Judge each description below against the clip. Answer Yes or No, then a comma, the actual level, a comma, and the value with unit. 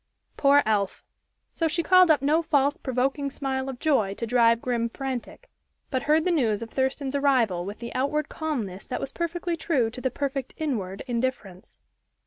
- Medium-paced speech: Yes, average, 175 wpm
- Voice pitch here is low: No, very high, 265 Hz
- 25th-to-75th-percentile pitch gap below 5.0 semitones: Yes, average, 4.3 semitones